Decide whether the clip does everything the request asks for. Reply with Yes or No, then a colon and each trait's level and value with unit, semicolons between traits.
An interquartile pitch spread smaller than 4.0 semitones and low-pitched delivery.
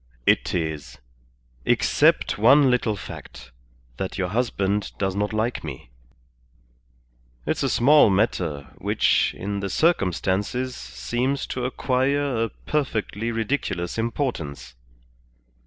No: wide, 5.6 semitones; low, 105 Hz